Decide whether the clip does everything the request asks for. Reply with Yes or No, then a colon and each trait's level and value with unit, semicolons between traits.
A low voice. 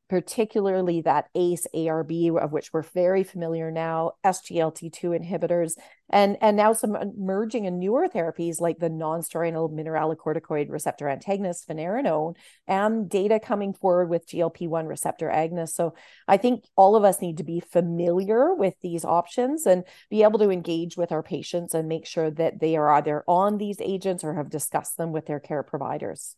No: medium, 170 Hz